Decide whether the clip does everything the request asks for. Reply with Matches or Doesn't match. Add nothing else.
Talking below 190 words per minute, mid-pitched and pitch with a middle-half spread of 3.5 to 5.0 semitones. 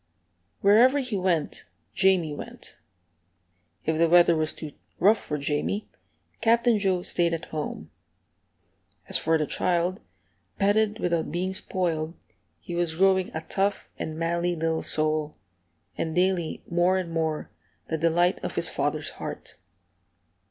Doesn't match